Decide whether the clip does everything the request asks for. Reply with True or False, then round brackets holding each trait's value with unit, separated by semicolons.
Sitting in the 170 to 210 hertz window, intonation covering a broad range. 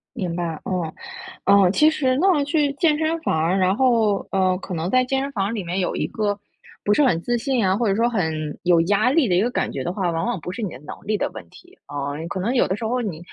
True (200 Hz; 6.1 semitones)